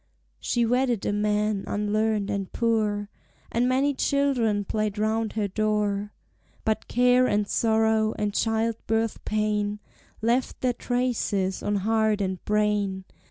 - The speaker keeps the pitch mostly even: Yes, narrow, 1.8 semitones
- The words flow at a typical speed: No, slow, 130 wpm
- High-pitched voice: Yes, high, 215 Hz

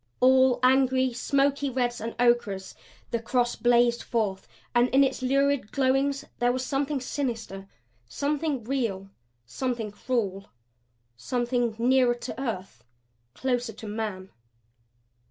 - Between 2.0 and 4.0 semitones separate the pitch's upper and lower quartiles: Yes, average, 2.7 semitones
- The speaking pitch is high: Yes, high, 245 Hz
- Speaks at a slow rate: Yes, slow, 115 wpm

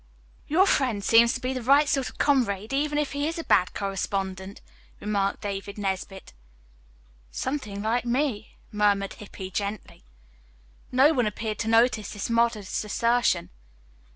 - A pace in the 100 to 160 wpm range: Yes, average, 145 wpm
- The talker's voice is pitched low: No, high, 220 Hz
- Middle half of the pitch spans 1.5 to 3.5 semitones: No, average, 4.5 semitones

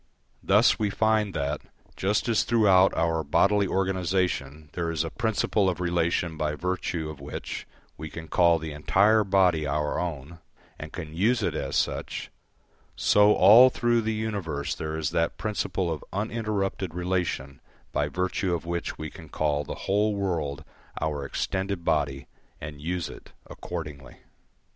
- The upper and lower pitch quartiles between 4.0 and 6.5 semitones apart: Yes, average, 4.3 semitones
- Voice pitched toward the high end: No, very low, 90 Hz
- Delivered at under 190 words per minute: Yes, average, 155 wpm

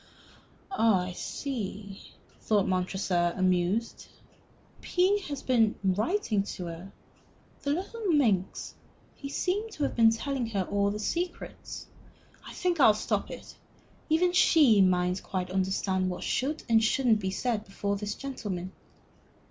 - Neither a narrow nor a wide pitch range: No, wide, 6.8 semitones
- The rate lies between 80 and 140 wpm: Yes, slow, 135 wpm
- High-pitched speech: Yes, high, 215 Hz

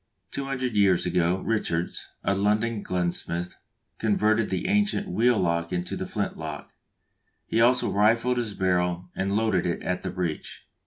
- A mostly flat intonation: No, average, 4.4 semitones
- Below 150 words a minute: No, average, 155 wpm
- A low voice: Yes, low, 100 Hz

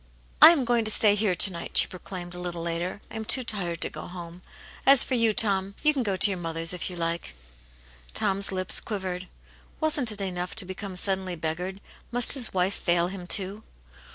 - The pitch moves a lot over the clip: No, average, 3.3 semitones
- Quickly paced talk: Yes, fast, 215 wpm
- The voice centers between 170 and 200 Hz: Yes, high, 190 Hz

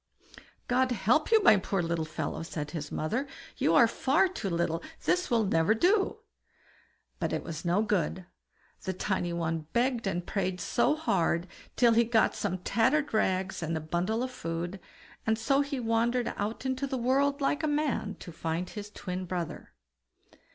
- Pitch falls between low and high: No, high, 210 Hz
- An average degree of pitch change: No, wide, 6.8 semitones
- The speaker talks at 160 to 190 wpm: Yes, average, 175 wpm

